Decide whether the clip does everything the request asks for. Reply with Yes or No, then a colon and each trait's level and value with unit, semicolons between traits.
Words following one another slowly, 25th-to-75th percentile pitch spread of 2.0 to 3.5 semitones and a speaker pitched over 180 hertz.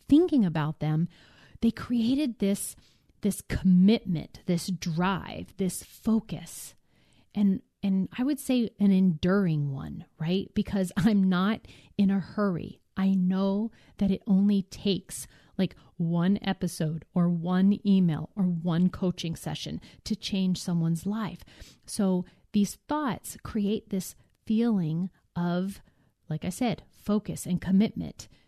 Yes: slow, 125 wpm; average, 2.8 semitones; high, 190 Hz